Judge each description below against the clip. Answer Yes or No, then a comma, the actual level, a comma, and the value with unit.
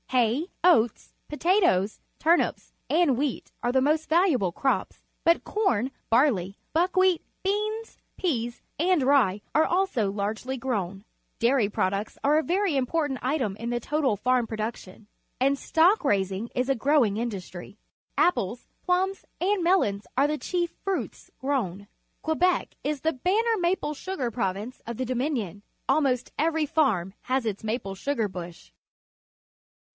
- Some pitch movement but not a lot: No, wide, 7.2 semitones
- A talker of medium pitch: No, very high, 265 Hz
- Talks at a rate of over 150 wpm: No, average, 140 wpm